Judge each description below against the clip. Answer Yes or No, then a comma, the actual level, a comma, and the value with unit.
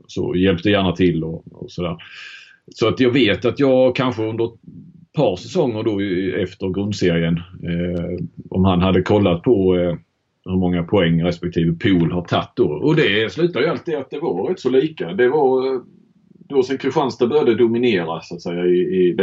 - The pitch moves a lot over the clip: Yes, wide, 6.6 semitones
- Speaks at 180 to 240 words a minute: Yes, average, 185 wpm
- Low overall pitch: Yes, very low, 95 Hz